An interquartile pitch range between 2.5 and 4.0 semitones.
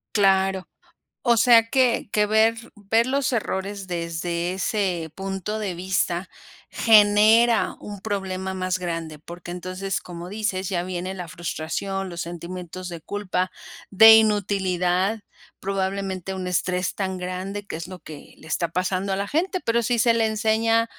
Yes: average, 2.8 semitones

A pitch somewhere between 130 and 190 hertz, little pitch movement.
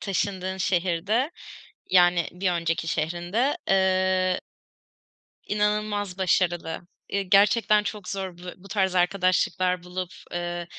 Yes: medium, 185 Hz; narrow, 2.1 semitones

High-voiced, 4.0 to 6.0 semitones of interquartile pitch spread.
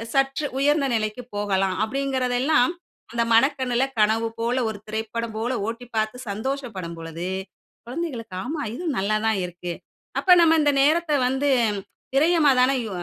Yes: high, 245 Hz; average, 4.3 semitones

